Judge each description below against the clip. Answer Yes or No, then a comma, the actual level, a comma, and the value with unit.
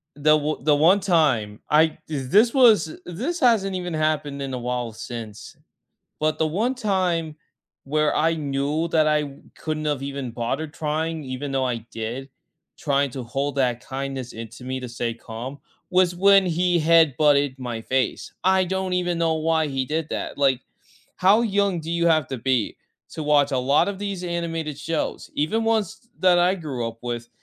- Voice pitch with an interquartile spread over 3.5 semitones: Yes, average, 4.8 semitones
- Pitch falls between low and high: Yes, medium, 155 Hz